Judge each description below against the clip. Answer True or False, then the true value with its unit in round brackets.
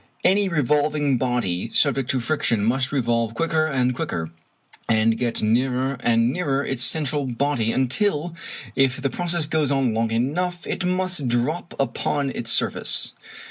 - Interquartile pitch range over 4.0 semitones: True (4.4 semitones)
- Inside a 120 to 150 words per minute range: True (145 wpm)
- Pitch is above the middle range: False (135 Hz)